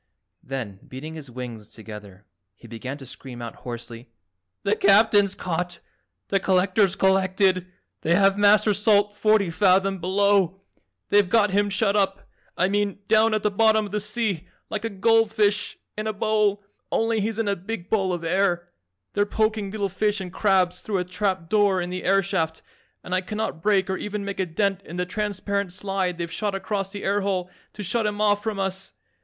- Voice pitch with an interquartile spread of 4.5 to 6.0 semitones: No, narrow, 2.5 semitones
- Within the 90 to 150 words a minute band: No, average, 190 wpm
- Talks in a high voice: Yes, high, 195 Hz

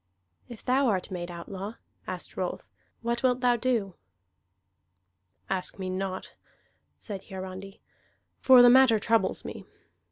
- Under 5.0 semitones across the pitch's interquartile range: Yes, average, 4.5 semitones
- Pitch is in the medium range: No, high, 210 Hz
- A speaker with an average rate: No, slow, 125 wpm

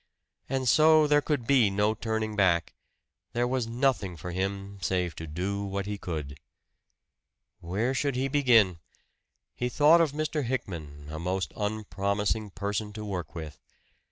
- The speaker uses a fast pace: No, average, 150 wpm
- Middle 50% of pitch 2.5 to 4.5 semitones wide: No, average, 5.3 semitones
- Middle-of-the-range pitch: No, low, 105 Hz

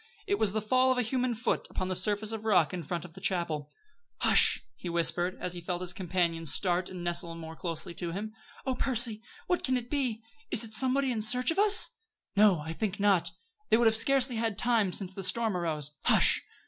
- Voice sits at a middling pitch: No, high, 205 Hz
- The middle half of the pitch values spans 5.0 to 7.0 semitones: Yes, average, 5.3 semitones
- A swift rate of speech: Yes, fast, 220 wpm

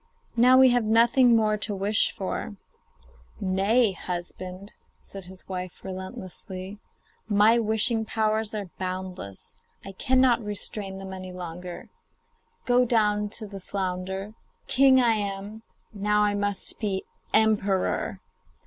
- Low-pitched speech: No, high, 205 Hz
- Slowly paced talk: Yes, slow, 120 wpm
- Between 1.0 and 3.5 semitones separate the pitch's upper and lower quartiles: Yes, average, 2.7 semitones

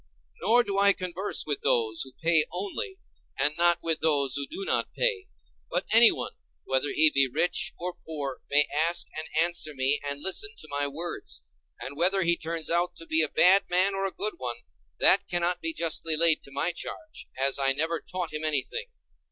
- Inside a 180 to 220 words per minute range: Yes, average, 200 wpm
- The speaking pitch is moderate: Yes, medium, 165 Hz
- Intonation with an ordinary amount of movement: Yes, average, 4.2 semitones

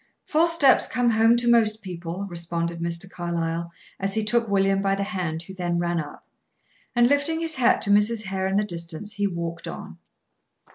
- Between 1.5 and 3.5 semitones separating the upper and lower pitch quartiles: No, average, 4.8 semitones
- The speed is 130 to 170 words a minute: No, average, 190 wpm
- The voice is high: Yes, high, 195 Hz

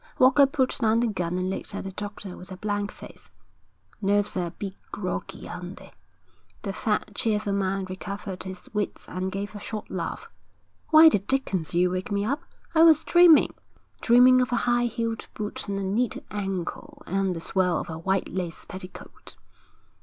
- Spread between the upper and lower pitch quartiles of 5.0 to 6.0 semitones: No, average, 3.7 semitones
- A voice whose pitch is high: Yes, high, 200 Hz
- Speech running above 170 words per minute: Yes, average, 185 wpm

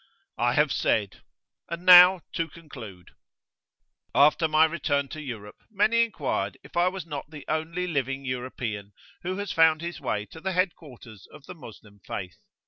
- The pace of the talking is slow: No, average, 165 wpm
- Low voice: No, medium, 155 Hz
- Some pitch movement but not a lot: No, wide, 5.9 semitones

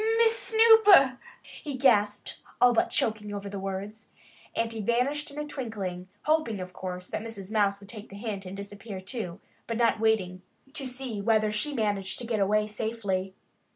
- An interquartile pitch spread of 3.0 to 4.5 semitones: Yes, average, 3.7 semitones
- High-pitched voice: Yes, high, 215 Hz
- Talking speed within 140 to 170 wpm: No, average, 180 wpm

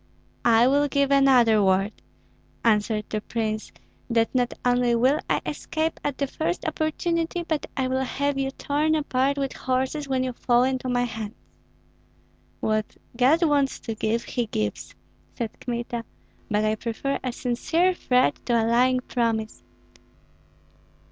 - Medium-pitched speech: No, very high, 255 Hz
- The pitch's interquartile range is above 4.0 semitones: No, average, 3.5 semitones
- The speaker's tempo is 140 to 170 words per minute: Yes, average, 150 wpm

